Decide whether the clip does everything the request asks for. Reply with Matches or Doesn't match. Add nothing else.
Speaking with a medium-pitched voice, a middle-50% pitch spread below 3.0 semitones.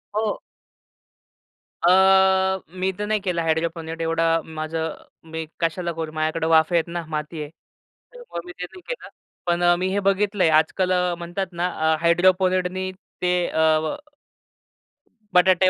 Matches